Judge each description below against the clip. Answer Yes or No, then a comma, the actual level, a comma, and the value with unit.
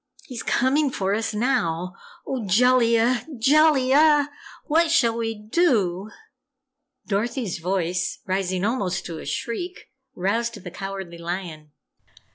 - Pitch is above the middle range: Yes, high, 225 Hz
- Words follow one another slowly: Yes, slow, 110 wpm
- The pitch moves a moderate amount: No, wide, 5.7 semitones